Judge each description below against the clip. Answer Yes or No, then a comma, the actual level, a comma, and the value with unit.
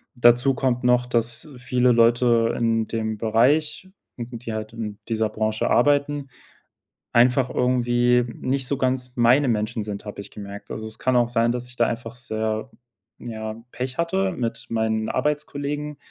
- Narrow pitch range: Yes, narrow, 2.3 semitones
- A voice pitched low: Yes, low, 120 Hz